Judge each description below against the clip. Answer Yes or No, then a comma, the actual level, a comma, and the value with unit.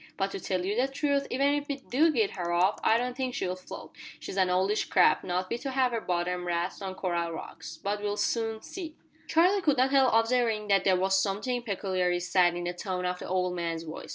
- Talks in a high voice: Yes, high, 195 Hz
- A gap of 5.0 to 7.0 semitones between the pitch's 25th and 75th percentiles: Yes, wide, 5.6 semitones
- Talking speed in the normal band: No, fast, 235 wpm